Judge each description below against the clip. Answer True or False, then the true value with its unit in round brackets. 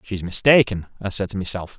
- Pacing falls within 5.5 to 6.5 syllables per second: True (5.6 syllables/s)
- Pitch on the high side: False (100 Hz)